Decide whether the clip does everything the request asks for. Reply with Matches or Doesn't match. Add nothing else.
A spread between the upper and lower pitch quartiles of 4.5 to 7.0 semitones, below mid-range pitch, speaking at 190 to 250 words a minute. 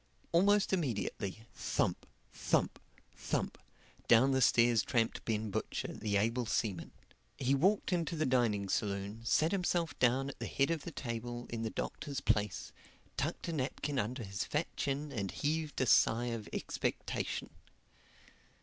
Doesn't match